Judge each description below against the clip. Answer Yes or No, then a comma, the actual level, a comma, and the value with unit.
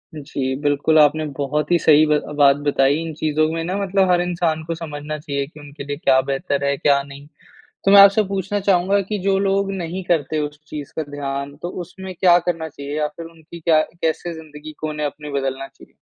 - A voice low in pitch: No, medium, 155 Hz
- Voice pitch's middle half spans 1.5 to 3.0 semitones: No, average, 3.4 semitones